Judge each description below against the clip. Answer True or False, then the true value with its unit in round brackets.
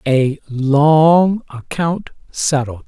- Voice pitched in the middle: True (150 Hz)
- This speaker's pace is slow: True (85 wpm)